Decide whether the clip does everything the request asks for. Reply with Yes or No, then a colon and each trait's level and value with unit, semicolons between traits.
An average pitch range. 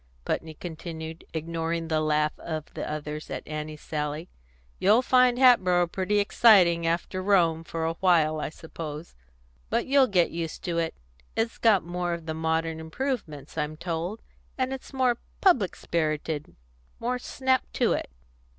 Yes: average, 4.3 semitones